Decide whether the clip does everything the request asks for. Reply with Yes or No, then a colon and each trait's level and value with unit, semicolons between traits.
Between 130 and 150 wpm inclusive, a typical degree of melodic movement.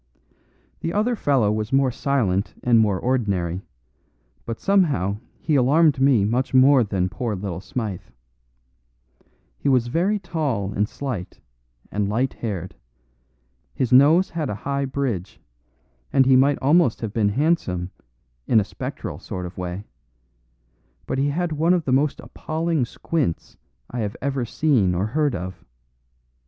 No: average, 145 wpm; wide, 6.2 semitones